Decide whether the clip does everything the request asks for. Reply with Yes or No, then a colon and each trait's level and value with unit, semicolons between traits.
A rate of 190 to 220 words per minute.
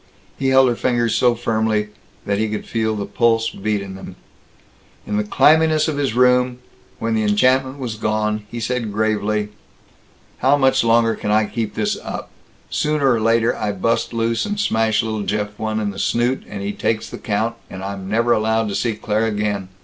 Yes: average, 195 wpm